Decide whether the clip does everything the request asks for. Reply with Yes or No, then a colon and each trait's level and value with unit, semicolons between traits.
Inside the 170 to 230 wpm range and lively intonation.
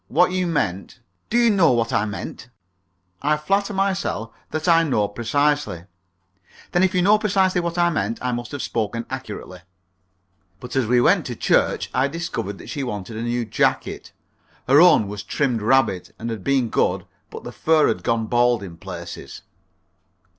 Yes: average, 180 wpm; wide, 7.4 semitones